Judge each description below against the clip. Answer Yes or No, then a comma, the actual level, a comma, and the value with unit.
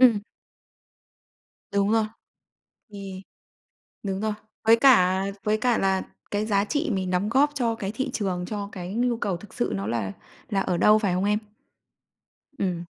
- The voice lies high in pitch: Yes, high, 205 Hz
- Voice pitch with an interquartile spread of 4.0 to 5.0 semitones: No, average, 3.1 semitones